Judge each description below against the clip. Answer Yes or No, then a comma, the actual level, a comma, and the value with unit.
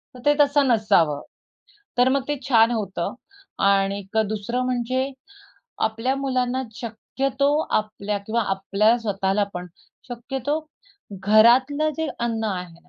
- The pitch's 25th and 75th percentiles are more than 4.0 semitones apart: Yes, average, 4.4 semitones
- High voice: Yes, high, 230 Hz